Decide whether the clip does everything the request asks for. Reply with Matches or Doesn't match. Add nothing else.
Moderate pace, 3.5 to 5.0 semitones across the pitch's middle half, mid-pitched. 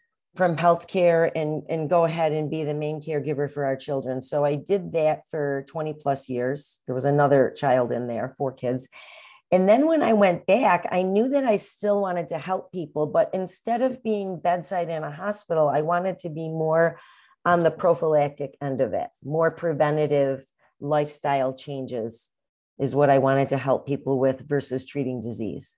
Matches